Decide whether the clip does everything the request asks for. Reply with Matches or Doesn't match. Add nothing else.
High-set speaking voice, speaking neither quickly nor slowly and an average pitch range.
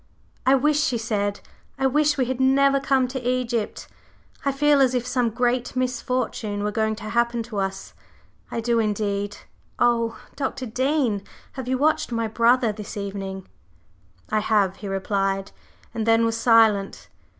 Matches